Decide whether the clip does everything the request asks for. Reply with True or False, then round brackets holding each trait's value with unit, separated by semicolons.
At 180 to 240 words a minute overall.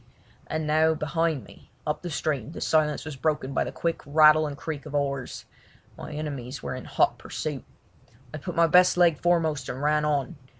True (190 wpm)